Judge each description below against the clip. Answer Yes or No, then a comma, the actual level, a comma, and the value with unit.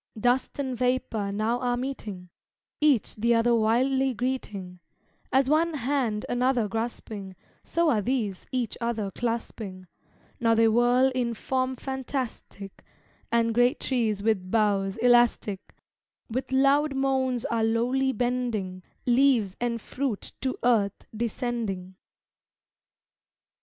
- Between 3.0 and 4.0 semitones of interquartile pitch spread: Yes, average, 3.3 semitones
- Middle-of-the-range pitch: No, high, 240 Hz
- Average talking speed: No, slow, 115 wpm